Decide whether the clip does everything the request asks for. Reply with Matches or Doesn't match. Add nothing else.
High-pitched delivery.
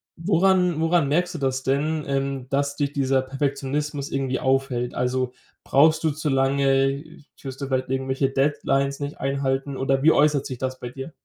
Doesn't match